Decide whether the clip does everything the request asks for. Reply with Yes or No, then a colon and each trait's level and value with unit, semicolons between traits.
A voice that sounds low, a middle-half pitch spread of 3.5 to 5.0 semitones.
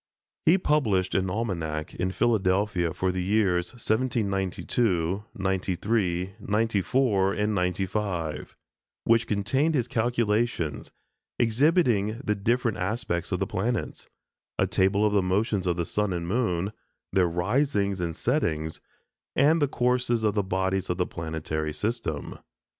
Yes: low, 100 Hz; average, 4.2 semitones